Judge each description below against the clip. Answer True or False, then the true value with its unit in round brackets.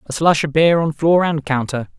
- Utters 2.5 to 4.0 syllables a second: False (5.0 syllables/s)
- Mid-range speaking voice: True (155 Hz)